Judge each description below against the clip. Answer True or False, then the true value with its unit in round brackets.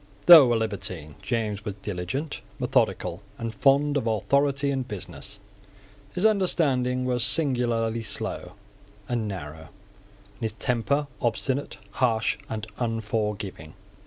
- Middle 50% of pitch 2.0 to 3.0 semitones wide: False (4.5 semitones)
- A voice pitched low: True (115 Hz)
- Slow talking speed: True (115 wpm)